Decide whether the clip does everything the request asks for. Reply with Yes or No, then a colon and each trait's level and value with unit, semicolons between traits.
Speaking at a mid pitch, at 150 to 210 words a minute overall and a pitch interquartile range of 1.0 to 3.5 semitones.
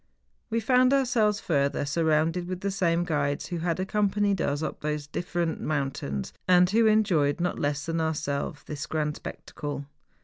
No: medium, 165 Hz; average, 170 wpm; average, 4.7 semitones